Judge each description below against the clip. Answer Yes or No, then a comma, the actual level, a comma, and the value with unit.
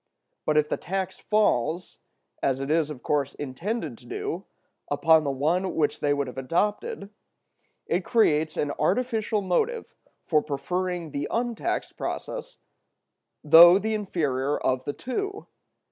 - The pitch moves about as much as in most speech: No, wide, 6.6 semitones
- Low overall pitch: No, medium, 170 Hz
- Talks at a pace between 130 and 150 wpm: Yes, average, 140 wpm